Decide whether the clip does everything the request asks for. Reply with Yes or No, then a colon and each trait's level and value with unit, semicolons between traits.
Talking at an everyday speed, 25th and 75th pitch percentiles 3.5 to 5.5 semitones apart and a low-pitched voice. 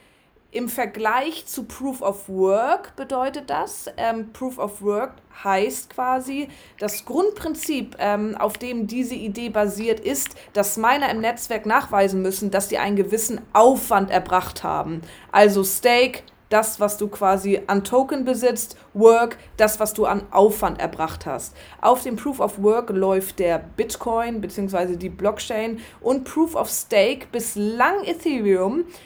No: average, 145 wpm; average, 3.9 semitones; high, 220 Hz